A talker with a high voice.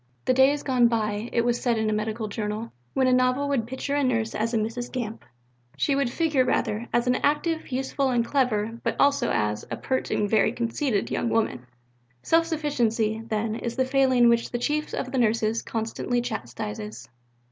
Yes: high, 240 Hz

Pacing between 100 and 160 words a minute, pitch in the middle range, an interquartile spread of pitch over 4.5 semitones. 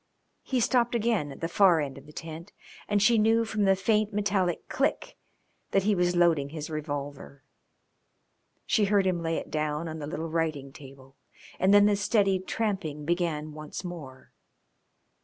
No: average, 170 wpm; medium, 175 Hz; average, 5.1 semitones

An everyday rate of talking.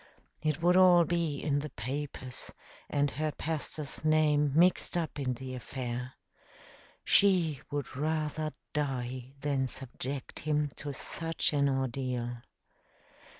No: slow, 120 wpm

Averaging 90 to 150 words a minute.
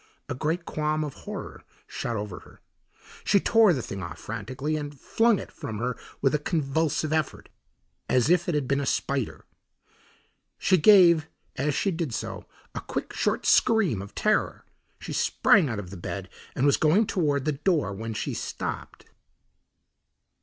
No: average, 165 wpm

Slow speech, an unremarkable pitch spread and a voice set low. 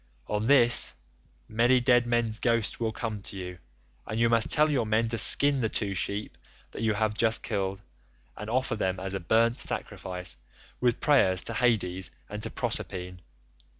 No: average, 175 wpm; average, 3.3 semitones; low, 110 Hz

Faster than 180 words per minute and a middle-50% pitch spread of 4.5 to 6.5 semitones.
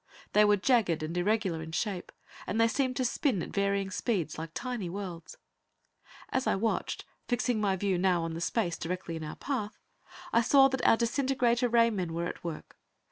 Yes: average, 190 wpm; average, 5.3 semitones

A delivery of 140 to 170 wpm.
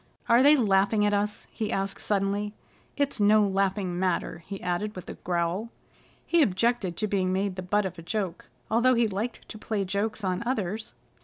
No: average, 185 wpm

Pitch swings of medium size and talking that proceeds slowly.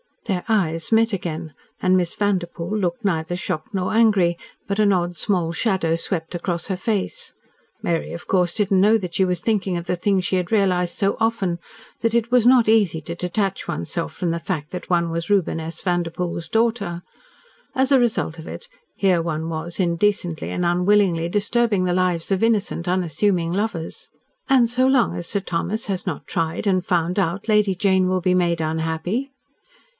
No: average, 3.5 semitones; average, 190 wpm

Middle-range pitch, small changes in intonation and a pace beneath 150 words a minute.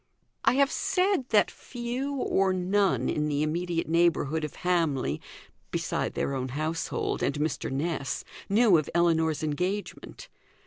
No: medium, 170 Hz; average, 5.1 semitones; slow, 135 wpm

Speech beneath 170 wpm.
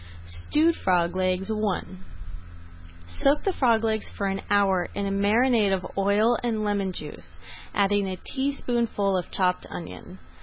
Yes: average, 145 wpm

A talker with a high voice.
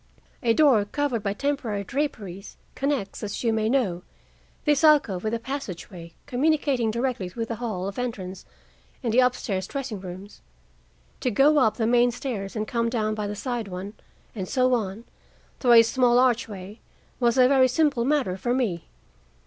Yes: high, 230 Hz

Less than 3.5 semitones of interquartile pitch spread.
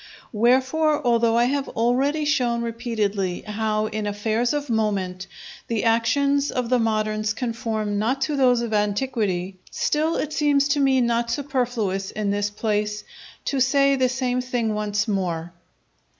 No: average, 3.8 semitones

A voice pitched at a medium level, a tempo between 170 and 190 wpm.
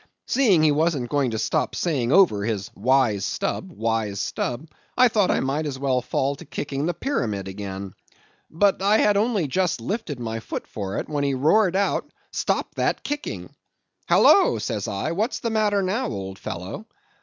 Yes: medium, 145 Hz; average, 180 wpm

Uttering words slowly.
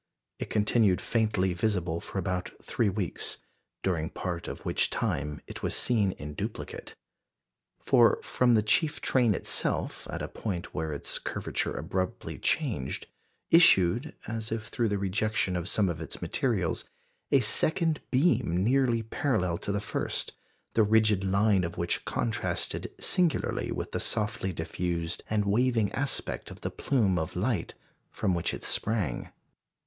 No: average, 150 wpm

